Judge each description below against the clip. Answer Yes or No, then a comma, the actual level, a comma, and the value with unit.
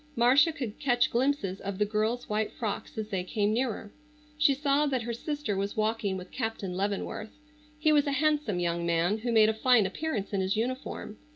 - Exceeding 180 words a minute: Yes, average, 195 wpm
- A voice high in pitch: Yes, high, 220 Hz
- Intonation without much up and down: No, average, 4.9 semitones